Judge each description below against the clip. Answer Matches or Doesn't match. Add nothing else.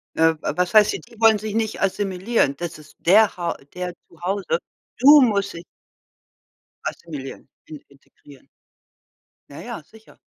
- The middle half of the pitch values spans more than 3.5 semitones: Matches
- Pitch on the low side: Doesn't match